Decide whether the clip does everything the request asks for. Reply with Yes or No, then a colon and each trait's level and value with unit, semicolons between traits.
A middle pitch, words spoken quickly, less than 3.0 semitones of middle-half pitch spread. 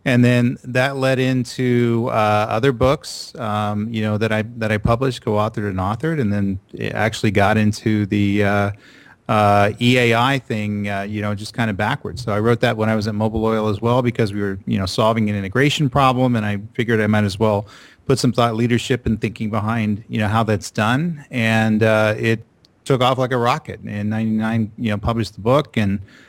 No: low, 110 Hz; fast, 215 wpm; narrow, 2.6 semitones